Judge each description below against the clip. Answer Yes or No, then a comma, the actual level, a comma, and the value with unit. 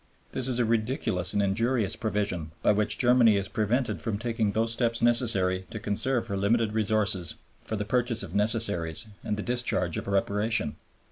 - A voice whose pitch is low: Yes, low, 110 Hz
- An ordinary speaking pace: Yes, average, 175 wpm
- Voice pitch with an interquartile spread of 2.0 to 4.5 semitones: Yes, average, 2.8 semitones